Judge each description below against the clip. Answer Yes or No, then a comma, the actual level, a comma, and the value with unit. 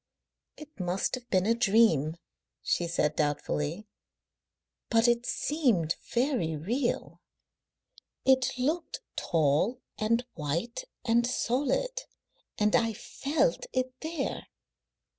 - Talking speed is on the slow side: Yes, slow, 105 wpm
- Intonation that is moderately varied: No, wide, 7.1 semitones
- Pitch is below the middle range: No, high, 235 Hz